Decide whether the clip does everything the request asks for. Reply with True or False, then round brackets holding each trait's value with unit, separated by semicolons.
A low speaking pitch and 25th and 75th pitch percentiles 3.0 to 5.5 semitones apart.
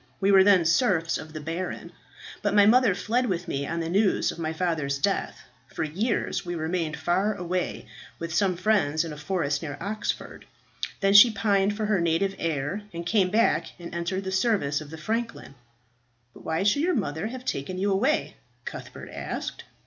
False (185 Hz; 4.1 semitones)